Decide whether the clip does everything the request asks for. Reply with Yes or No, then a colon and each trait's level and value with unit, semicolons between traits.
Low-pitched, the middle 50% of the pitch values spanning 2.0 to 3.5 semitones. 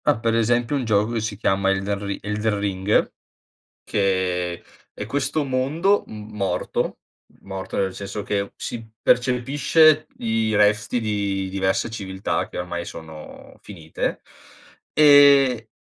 No: low, 105 Hz; average, 4.0 semitones